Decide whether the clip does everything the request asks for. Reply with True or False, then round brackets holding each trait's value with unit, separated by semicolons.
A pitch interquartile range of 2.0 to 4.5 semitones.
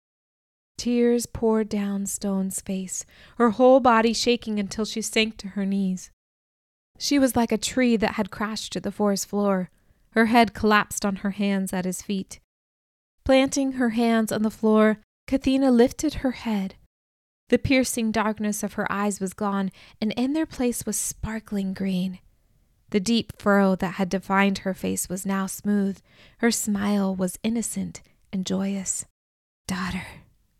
True (3.0 semitones)